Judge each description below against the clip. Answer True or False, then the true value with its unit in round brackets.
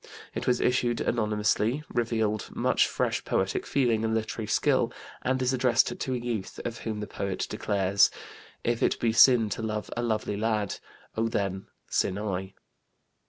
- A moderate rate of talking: True (165 wpm)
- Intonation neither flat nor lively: False (2.2 semitones)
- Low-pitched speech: True (110 Hz)